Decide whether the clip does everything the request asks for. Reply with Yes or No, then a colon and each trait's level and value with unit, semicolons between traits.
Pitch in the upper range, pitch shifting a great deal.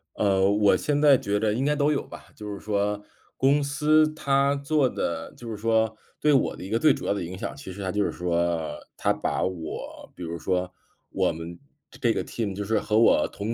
No: low, 105 Hz; wide, 6.5 semitones